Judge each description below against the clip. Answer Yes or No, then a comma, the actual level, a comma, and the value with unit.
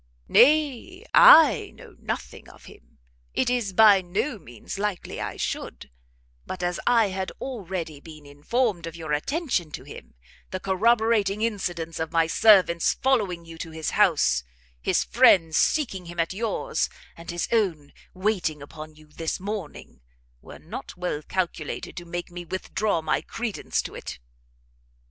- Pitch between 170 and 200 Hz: Yes, medium, 185 Hz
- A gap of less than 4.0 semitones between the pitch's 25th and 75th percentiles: No, average, 5.2 semitones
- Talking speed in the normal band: Yes, average, 150 wpm